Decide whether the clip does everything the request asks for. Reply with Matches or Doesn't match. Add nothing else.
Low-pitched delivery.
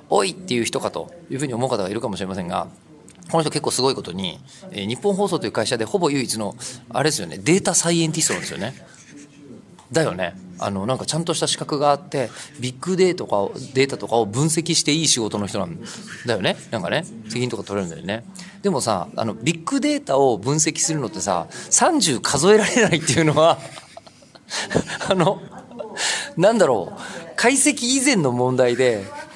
Doesn't match